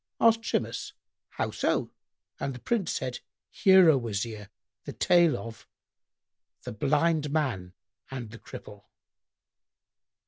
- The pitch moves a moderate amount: No, wide, 7.0 semitones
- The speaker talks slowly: Yes, slow, 115 wpm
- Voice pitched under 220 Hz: Yes, low, 135 Hz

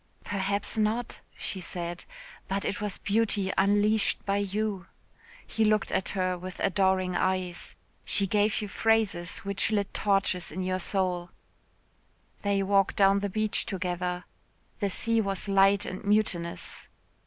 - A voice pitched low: No, high, 195 Hz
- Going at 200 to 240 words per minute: No, average, 140 wpm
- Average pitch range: No, narrow, 1.9 semitones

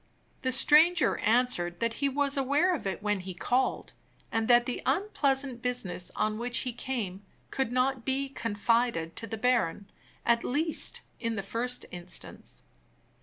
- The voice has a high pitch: Yes, high, 245 Hz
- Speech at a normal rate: Yes, average, 155 wpm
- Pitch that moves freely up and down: No, average, 3.9 semitones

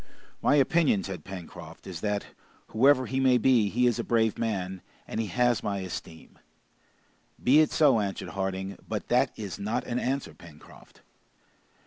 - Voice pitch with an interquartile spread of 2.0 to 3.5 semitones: No, average, 4.7 semitones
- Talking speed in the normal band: Yes, average, 160 wpm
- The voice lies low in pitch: Yes, low, 110 Hz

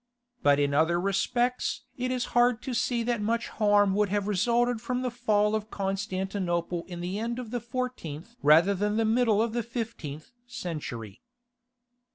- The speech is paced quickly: No, average, 170 wpm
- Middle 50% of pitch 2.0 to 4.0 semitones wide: No, average, 4.7 semitones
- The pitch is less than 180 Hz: No, high, 210 Hz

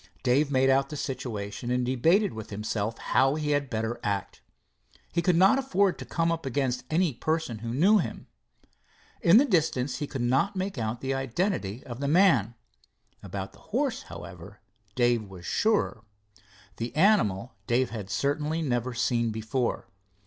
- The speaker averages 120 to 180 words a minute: Yes, average, 165 wpm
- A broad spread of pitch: Yes, wide, 5.8 semitones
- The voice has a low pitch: Yes, low, 130 Hz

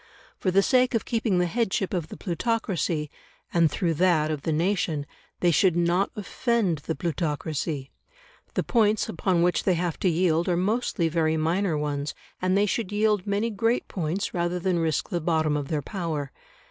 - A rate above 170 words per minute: Yes, average, 180 wpm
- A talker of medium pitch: Yes, medium, 175 Hz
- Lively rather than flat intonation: No, average, 4.0 semitones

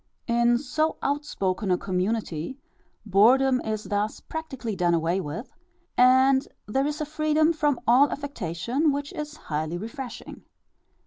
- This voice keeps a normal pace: No, slow, 130 wpm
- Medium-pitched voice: No, high, 245 Hz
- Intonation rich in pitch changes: Yes, wide, 6.5 semitones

